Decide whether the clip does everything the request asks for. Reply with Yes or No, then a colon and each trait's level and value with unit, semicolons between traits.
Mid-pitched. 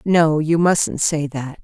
Yes: medium, 155 Hz